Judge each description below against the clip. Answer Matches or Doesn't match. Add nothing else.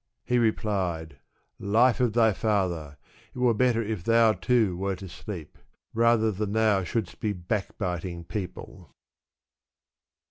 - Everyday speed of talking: Doesn't match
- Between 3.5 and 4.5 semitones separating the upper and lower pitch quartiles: Matches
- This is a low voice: Matches